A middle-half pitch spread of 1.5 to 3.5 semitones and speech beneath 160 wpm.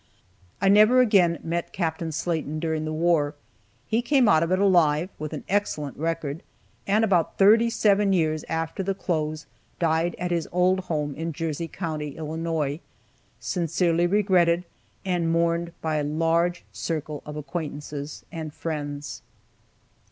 Yes: average, 2.7 semitones; average, 145 wpm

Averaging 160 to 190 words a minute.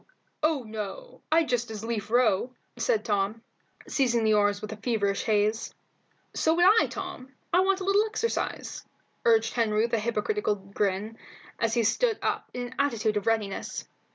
Yes: average, 165 wpm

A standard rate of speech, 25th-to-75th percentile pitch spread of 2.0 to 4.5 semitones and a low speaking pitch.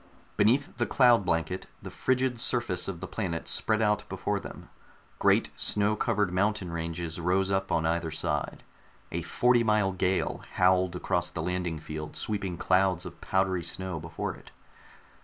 Yes: average, 160 wpm; average, 3.5 semitones; very low, 95 Hz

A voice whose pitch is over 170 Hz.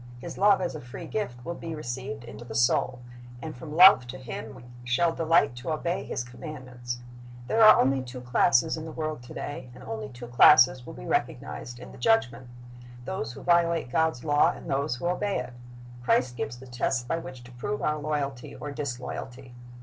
No: low, 130 Hz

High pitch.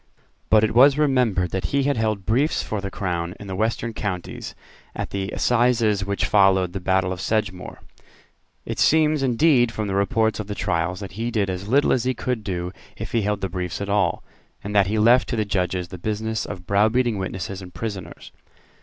No: low, 105 Hz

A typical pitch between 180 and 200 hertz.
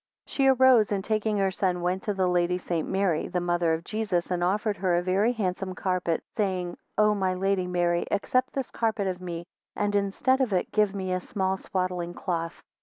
Yes: high, 190 Hz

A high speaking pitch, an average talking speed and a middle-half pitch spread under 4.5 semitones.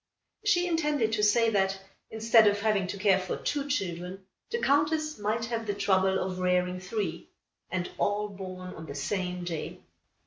Yes: high, 205 Hz; average, 170 wpm; average, 3.7 semitones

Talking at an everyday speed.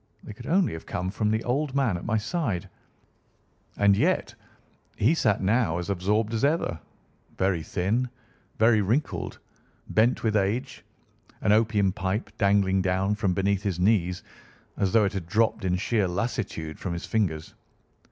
Yes: average, 160 wpm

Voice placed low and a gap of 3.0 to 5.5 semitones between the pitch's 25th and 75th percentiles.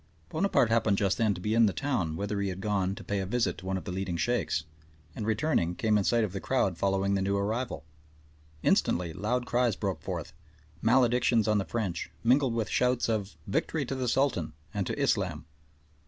Yes: low, 105 Hz; average, 4.0 semitones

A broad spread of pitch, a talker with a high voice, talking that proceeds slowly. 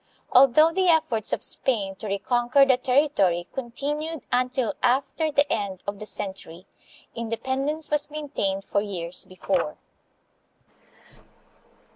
Yes: wide, 6.3 semitones; high, 245 Hz; slow, 120 wpm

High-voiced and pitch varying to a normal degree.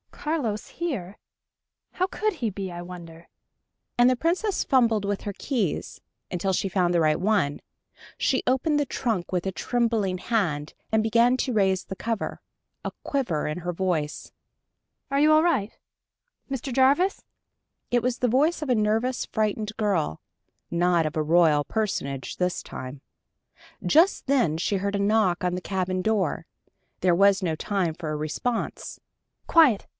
No: high, 205 Hz; wide, 5.9 semitones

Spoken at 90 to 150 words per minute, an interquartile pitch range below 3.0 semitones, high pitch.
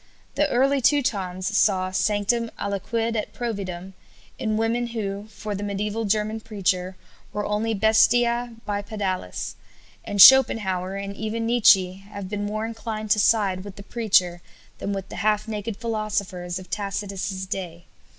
Yes: average, 140 wpm; narrow, 2.6 semitones; high, 210 Hz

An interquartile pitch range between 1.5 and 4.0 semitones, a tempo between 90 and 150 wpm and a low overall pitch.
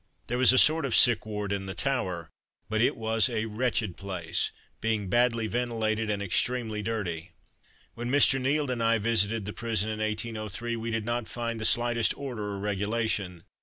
No: narrow, 2.4 semitones; average, 180 wpm; low, 110 Hz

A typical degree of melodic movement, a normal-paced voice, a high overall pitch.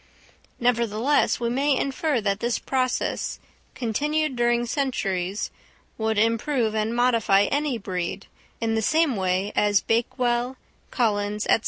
No: average, 3.5 semitones; slow, 125 wpm; high, 235 Hz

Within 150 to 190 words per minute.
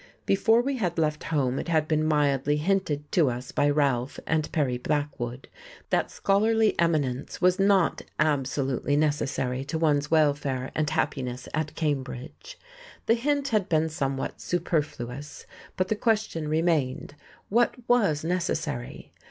No: slow, 135 wpm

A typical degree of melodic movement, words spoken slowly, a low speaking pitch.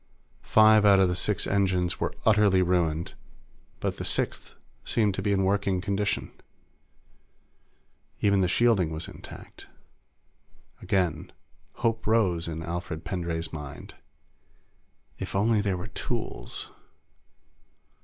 Yes: average, 3.1 semitones; slow, 115 wpm; very low, 95 Hz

